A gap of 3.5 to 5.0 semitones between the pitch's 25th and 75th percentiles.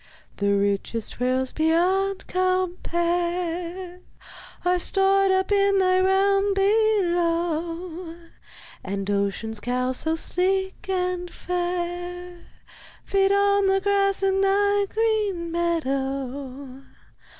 No: average, 3.1 semitones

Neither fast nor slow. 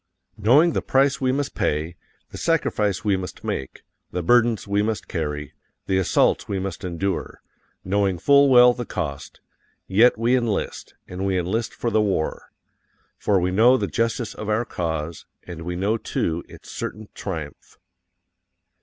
Yes: average, 160 wpm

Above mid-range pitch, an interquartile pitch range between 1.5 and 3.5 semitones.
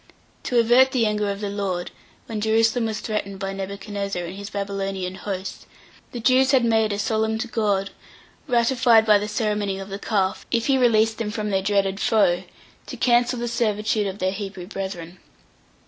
Yes: high, 210 Hz; narrow, 2.6 semitones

